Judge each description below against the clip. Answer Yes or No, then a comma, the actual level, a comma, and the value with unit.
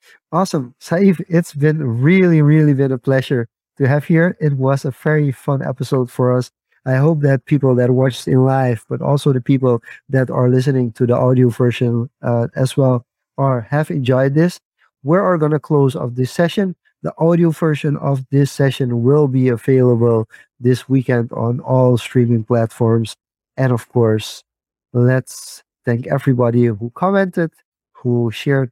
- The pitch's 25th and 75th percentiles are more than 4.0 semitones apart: No, average, 3.3 semitones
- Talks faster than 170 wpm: No, average, 165 wpm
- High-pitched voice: No, low, 135 Hz